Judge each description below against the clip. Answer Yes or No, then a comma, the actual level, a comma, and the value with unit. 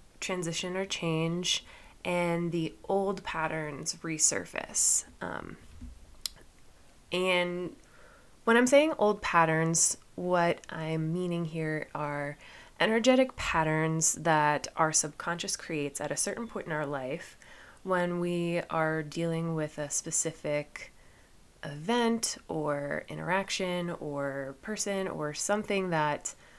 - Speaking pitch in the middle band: Yes, medium, 165 Hz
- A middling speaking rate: No, slow, 110 wpm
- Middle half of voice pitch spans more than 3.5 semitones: No, average, 3.2 semitones